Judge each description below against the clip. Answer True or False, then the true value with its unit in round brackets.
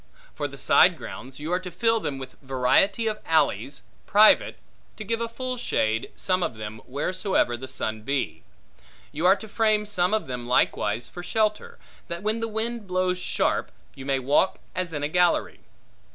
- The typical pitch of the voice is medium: True (180 Hz)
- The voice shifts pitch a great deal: True (8.1 semitones)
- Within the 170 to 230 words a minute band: True (180 wpm)